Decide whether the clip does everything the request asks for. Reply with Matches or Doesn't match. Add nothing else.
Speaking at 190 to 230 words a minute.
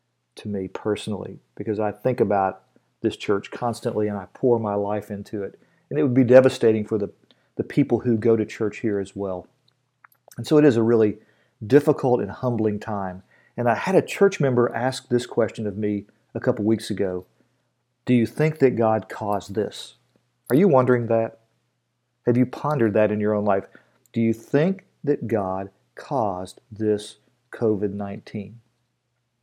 Doesn't match